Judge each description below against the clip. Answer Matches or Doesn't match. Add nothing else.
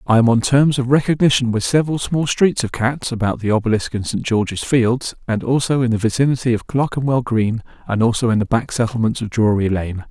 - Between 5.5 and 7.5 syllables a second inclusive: Matches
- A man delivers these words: Matches